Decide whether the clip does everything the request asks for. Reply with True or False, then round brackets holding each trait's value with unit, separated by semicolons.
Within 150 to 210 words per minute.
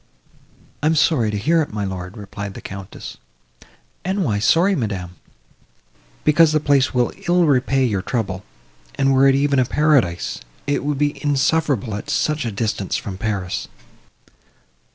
True (155 wpm)